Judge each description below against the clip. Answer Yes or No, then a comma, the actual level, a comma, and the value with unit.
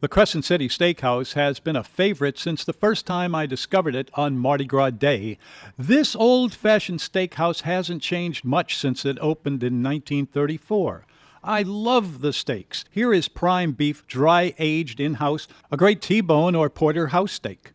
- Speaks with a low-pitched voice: No, medium, 160 Hz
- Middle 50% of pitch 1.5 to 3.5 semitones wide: No, average, 4.3 semitones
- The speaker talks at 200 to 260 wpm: No, average, 160 wpm